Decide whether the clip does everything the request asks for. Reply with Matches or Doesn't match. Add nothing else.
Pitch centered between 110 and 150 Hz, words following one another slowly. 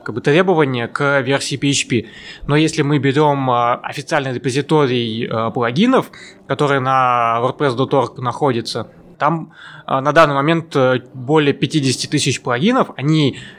Matches